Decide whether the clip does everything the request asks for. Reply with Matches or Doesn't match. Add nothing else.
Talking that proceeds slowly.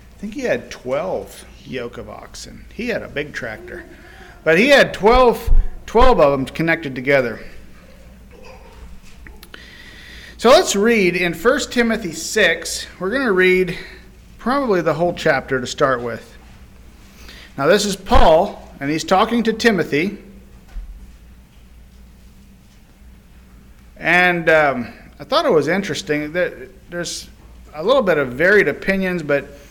Matches